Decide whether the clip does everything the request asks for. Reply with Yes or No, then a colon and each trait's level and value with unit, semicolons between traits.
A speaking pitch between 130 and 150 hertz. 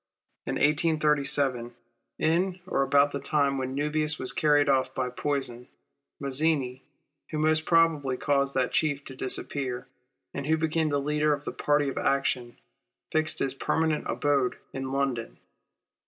Yes: medium, 140 Hz